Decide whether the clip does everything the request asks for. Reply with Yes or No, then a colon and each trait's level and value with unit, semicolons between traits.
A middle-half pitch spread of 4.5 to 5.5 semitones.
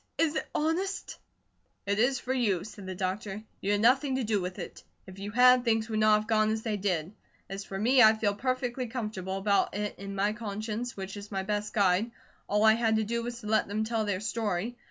No: average, 2.8 semitones